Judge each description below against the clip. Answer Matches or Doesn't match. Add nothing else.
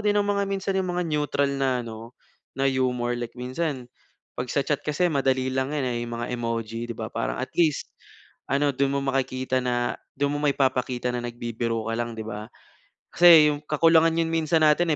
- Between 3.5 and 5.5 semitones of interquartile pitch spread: Matches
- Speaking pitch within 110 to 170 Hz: Matches